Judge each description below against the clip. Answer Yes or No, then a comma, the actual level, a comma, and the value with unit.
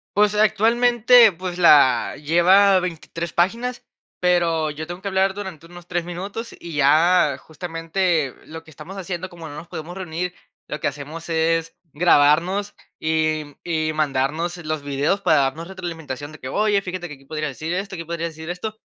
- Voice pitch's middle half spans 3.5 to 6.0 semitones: No, average, 3.1 semitones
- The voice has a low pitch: No, medium, 170 Hz